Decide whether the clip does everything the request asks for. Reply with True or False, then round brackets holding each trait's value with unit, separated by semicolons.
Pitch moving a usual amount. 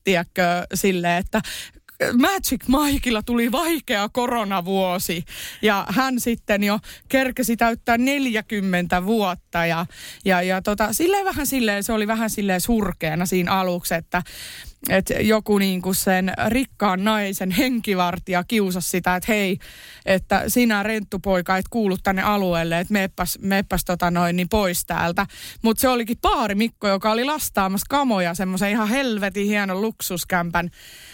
True (3.6 semitones)